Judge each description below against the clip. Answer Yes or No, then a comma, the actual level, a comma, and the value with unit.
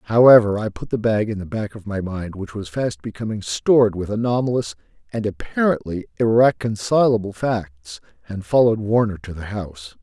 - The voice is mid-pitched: No, low, 105 Hz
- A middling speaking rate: Yes, average, 170 wpm